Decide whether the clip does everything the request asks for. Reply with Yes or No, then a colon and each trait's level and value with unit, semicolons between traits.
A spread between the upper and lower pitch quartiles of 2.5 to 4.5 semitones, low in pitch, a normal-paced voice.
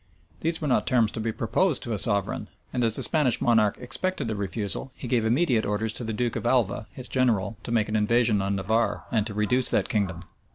No: average, 2.8 semitones; low, 115 Hz; fast, 230 wpm